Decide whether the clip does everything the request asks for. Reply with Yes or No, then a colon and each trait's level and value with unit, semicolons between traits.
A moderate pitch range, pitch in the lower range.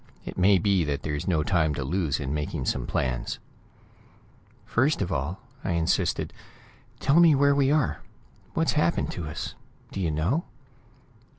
No: wide, 7.6 semitones; very low, 85 Hz